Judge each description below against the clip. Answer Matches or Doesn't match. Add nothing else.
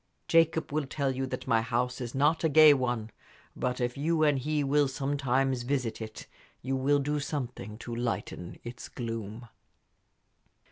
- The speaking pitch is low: Matches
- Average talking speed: Matches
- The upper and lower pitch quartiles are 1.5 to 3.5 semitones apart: Matches